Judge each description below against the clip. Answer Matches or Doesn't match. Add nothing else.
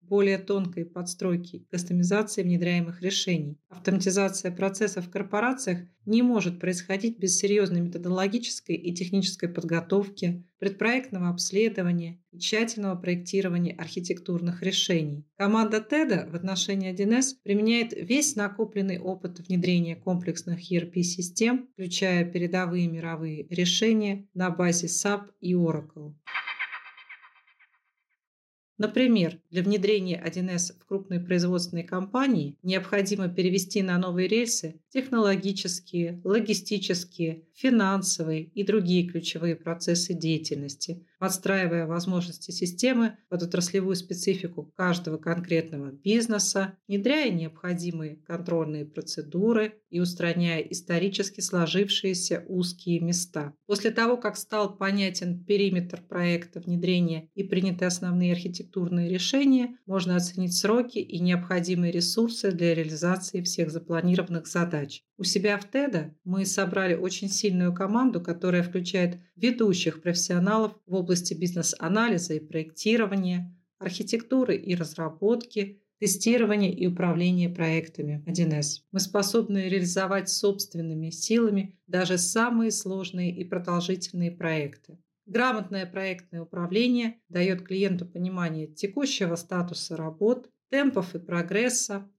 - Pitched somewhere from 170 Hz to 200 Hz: Matches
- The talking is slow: Matches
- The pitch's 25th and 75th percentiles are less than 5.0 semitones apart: Matches